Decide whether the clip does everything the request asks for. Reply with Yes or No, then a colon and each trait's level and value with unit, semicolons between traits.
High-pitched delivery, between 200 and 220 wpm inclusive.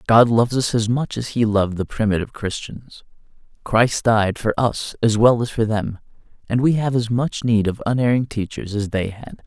No: low, 115 Hz; fast, 205 wpm